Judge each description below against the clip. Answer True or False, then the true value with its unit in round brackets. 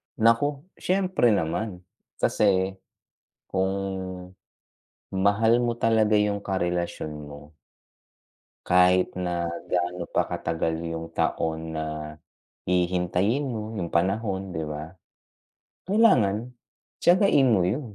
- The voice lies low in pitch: True (95 Hz)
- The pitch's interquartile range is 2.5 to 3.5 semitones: False (4.5 semitones)